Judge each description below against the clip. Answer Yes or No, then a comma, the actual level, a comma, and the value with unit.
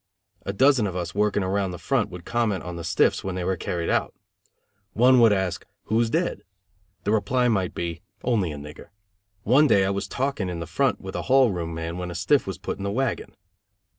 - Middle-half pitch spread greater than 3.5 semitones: Yes, average, 5.1 semitones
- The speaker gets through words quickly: Yes, fast, 220 wpm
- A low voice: Yes, low, 100 Hz